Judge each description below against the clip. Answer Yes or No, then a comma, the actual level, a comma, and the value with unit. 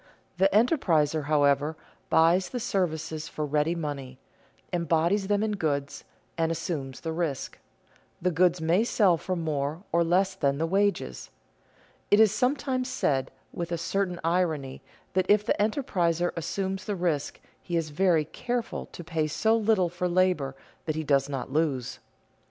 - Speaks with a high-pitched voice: No, medium, 170 Hz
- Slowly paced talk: No, average, 155 wpm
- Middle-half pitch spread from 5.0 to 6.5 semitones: No, average, 4.1 semitones